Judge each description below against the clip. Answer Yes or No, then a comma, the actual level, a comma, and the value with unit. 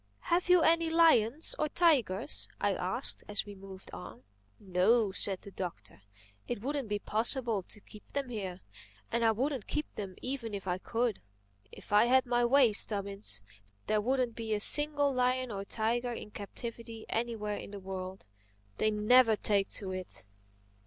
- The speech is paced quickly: No, average, 165 wpm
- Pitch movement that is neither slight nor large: Yes, average, 4.2 semitones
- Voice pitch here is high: Yes, high, 225 Hz